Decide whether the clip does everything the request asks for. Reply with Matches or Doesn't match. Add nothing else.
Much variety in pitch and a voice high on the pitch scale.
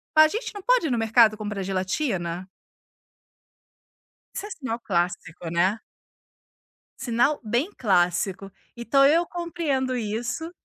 Matches